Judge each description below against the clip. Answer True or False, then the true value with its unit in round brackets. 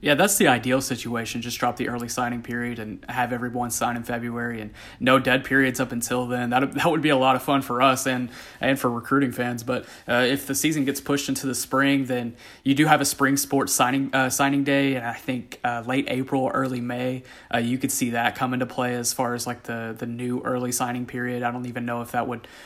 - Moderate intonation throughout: False (2.0 semitones)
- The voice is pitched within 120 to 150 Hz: True (125 Hz)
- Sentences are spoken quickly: True (245 wpm)